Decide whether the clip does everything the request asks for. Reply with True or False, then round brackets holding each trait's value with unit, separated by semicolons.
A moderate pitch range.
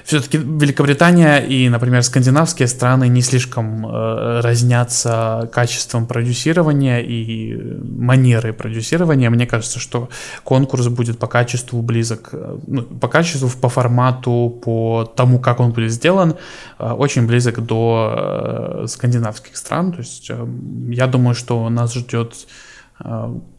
False (2.0 semitones)